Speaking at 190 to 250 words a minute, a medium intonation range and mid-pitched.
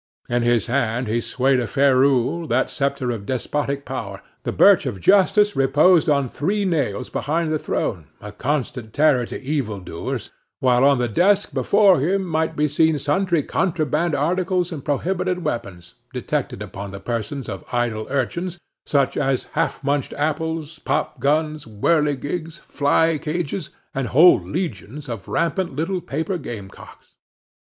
No: average, 150 wpm; average, 4.9 semitones; medium, 145 Hz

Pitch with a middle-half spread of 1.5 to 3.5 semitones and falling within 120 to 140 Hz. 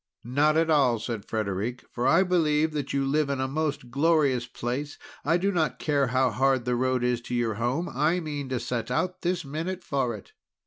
No: average, 4.1 semitones; low, 135 Hz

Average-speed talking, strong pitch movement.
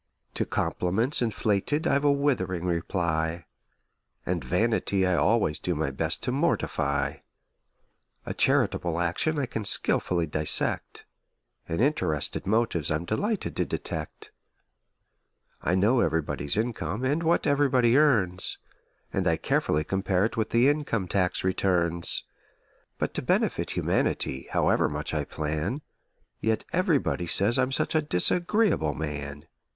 No: slow, 130 wpm; wide, 7.7 semitones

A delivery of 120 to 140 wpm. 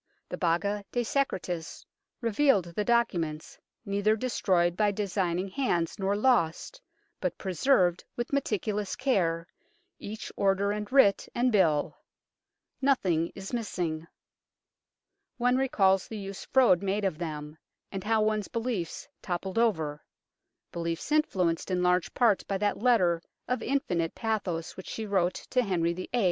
Yes: slow, 135 wpm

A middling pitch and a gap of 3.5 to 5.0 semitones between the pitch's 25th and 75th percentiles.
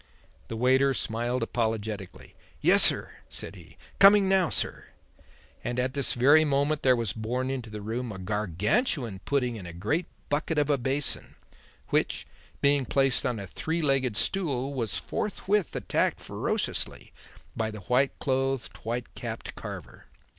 No: low, 130 Hz; average, 4.3 semitones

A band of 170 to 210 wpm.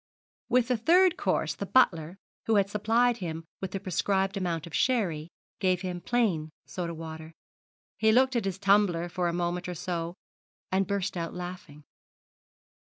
No: average, 160 wpm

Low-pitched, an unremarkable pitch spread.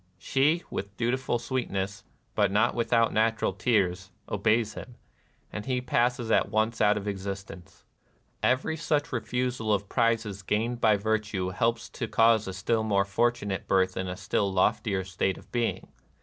Yes: low, 110 Hz; average, 3.4 semitones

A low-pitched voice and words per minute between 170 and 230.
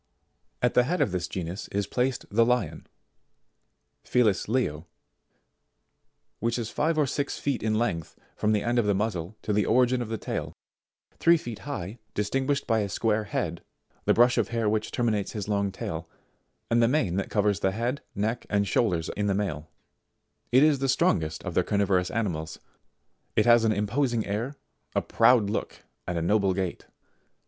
Yes: low, 110 Hz; average, 180 wpm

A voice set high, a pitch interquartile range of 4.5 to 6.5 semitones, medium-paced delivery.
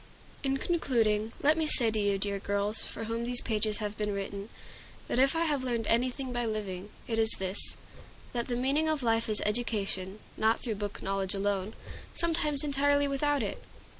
Yes: high, 225 Hz; average, 4.8 semitones; average, 185 wpm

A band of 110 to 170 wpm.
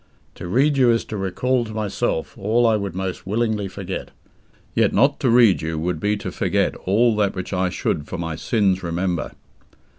No: average, 190 wpm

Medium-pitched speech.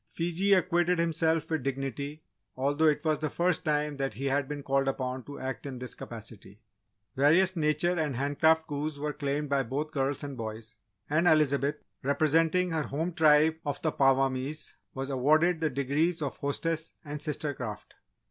Yes: medium, 150 Hz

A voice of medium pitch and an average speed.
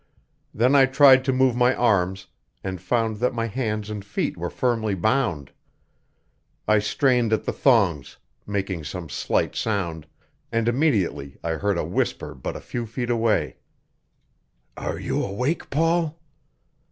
No: low, 110 Hz; average, 145 wpm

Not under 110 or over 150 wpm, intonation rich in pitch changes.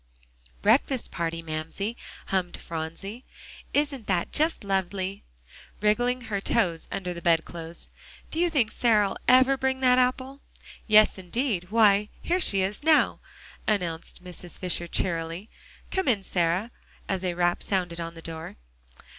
Yes: average, 140 wpm; wide, 5.9 semitones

